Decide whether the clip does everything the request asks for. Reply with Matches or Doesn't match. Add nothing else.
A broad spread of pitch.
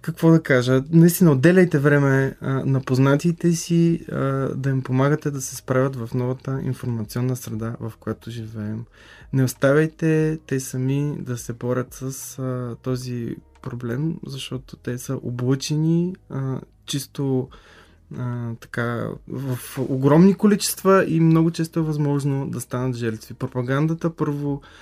Doesn't match